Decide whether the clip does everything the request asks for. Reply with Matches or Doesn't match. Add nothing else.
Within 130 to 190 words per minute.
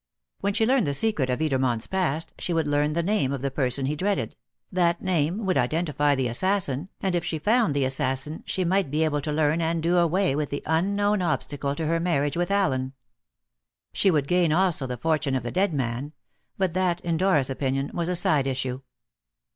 Doesn't match